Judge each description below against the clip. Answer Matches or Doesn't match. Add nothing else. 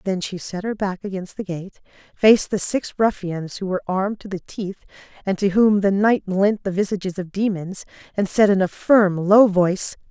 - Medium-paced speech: Doesn't match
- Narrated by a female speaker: Matches